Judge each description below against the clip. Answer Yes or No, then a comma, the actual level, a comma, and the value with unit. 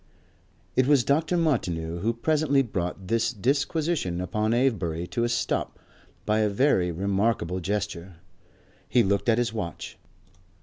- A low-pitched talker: Yes, low, 110 Hz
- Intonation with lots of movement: Yes, wide, 6.0 semitones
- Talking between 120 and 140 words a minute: Yes, slow, 135 wpm